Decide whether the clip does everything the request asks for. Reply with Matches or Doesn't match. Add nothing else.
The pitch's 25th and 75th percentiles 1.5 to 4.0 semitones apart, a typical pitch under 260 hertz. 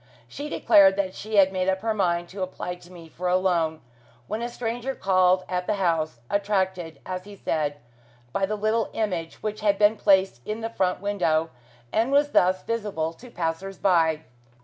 Matches